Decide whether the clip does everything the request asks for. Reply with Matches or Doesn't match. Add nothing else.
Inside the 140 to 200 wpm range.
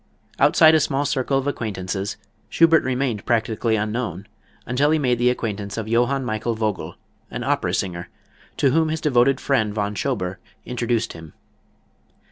Matches